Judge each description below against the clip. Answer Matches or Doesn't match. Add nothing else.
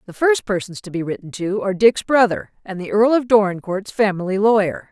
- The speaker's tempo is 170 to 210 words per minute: Matches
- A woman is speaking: Matches